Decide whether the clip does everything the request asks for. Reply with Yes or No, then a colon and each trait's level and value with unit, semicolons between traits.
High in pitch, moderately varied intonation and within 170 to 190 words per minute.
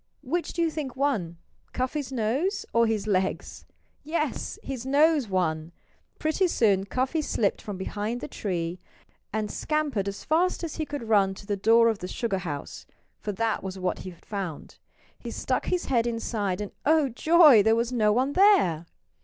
No: high, 230 Hz; wide, 6.7 semitones; average, 180 wpm